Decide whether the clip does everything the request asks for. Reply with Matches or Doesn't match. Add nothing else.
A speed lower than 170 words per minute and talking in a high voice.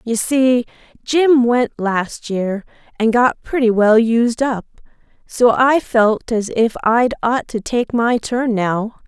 Matches